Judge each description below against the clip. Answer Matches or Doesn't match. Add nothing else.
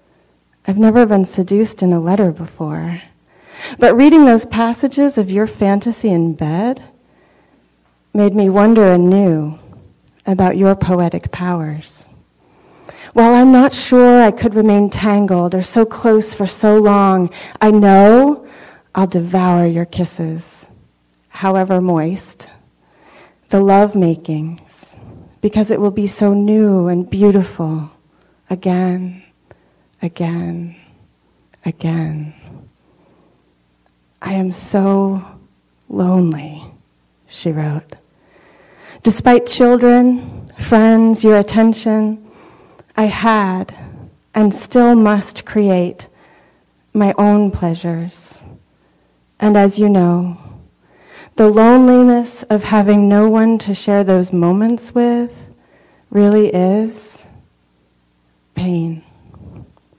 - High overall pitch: Matches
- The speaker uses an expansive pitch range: Doesn't match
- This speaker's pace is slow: Matches